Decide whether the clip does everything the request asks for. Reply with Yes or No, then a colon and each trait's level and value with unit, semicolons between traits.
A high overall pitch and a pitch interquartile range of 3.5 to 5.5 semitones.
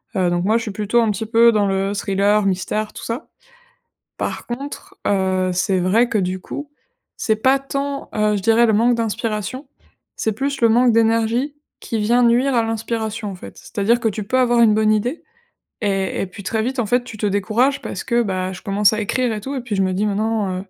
No: high, 220 Hz; average, 3.1 semitones